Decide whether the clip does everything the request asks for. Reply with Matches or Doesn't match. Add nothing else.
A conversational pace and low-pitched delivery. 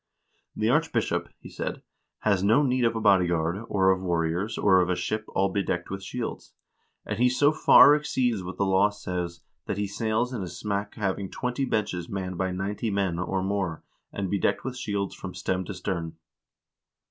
Matches